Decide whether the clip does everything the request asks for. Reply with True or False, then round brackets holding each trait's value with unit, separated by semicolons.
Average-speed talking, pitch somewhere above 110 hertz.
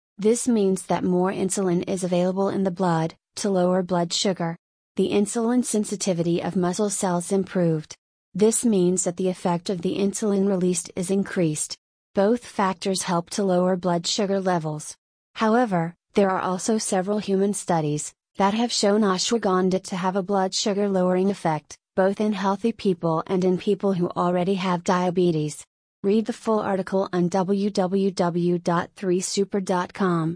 True (150 wpm; 190 Hz)